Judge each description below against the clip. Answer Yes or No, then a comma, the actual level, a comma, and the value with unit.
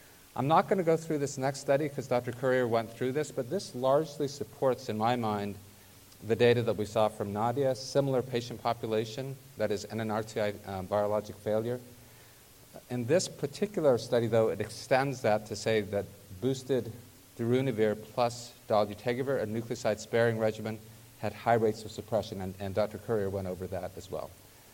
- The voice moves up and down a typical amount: Yes, average, 3.2 semitones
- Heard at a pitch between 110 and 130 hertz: Yes, low, 115 Hz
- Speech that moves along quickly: No, average, 170 wpm